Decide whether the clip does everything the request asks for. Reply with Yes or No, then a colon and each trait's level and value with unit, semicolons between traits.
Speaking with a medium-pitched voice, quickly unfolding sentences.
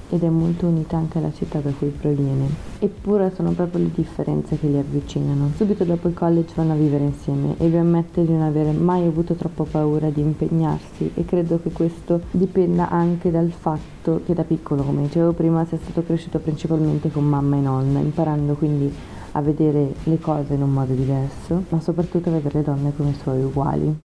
Yes: medium, 160 Hz; fast, 195 wpm